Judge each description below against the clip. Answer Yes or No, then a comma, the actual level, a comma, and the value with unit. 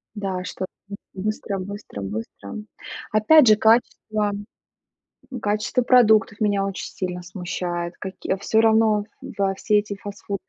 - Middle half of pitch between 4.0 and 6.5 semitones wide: No, narrow, 2.4 semitones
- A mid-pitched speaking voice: No, high, 205 Hz